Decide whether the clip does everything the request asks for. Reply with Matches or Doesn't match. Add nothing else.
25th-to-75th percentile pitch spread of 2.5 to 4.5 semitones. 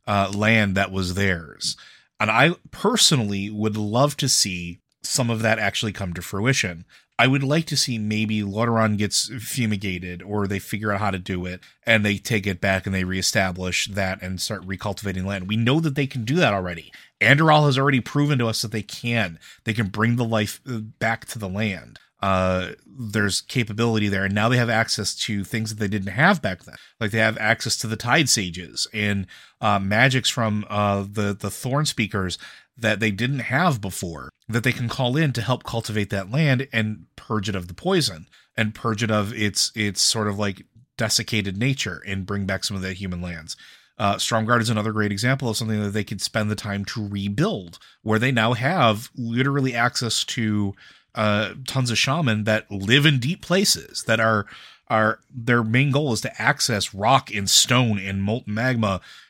Matches